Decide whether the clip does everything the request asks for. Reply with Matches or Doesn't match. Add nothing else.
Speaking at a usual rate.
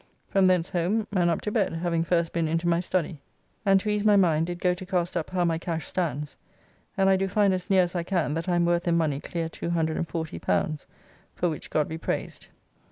Doesn't match